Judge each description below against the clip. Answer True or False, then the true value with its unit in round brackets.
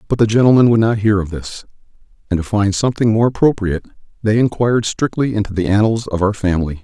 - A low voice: True (105 Hz)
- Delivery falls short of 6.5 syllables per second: False (6.6 syllables/s)